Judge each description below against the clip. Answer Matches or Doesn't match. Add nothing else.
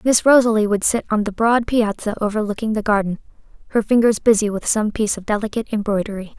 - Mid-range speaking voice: Doesn't match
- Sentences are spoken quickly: Doesn't match